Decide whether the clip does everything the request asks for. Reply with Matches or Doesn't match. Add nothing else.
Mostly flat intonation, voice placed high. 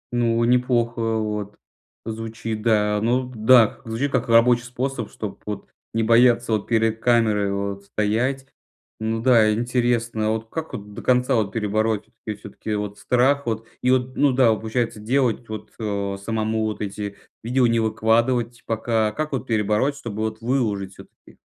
Doesn't match